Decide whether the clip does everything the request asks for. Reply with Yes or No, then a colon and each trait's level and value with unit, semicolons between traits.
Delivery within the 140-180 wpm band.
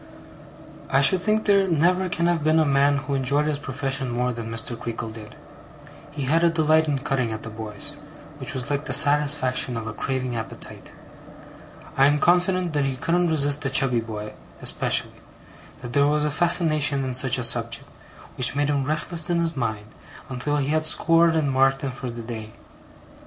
No: average, 190 wpm